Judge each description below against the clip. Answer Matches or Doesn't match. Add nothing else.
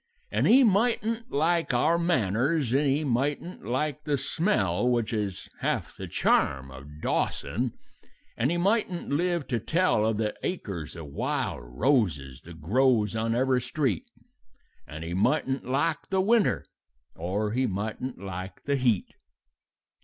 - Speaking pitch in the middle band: Doesn't match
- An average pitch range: Doesn't match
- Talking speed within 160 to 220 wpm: Doesn't match